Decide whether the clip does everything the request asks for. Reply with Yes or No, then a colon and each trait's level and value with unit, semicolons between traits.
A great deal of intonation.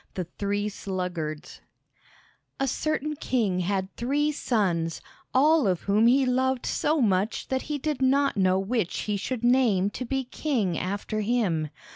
Yes: wide, 5.7 semitones